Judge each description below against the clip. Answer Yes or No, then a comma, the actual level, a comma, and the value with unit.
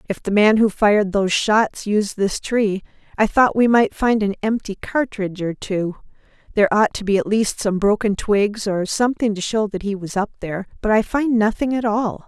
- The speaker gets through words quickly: Yes, fast, 215 wpm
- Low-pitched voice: No, high, 210 Hz